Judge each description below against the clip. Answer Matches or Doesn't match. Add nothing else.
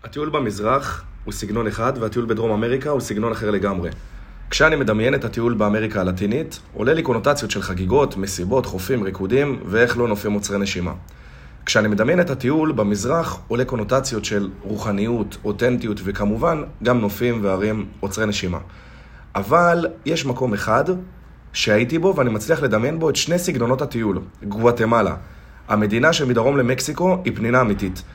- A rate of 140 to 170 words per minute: Matches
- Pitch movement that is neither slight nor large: Matches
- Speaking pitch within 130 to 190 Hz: Doesn't match